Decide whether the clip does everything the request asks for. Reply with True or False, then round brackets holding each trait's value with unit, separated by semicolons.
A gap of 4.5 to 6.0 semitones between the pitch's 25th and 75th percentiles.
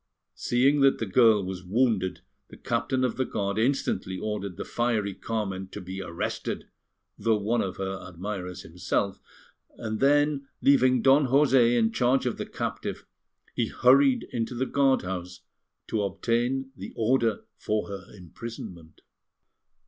True (5.0 semitones)